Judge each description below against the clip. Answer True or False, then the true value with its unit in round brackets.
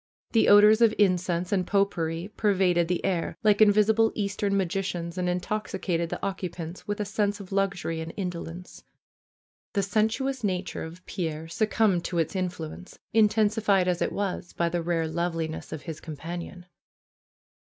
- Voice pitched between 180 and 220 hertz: True (185 Hz)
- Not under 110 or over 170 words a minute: True (155 wpm)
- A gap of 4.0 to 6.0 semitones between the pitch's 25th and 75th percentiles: False (3.2 semitones)